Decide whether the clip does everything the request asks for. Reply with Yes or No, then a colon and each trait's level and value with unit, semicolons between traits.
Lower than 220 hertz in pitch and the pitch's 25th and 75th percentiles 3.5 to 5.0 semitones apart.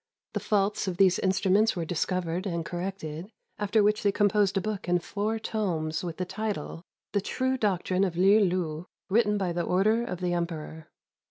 No: high, 190 Hz; average, 3.1 semitones